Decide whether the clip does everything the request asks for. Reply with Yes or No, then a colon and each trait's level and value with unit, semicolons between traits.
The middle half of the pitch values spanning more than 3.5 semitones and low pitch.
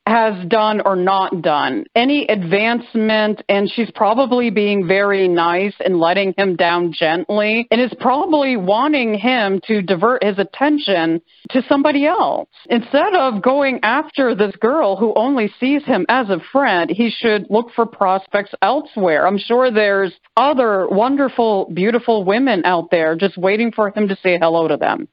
No: average, 4.1 semitones; high, 210 Hz